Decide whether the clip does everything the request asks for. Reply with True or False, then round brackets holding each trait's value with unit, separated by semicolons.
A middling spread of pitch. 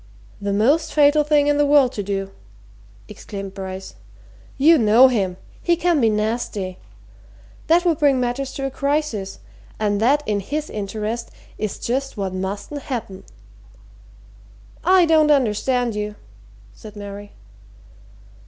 False (6.2 semitones)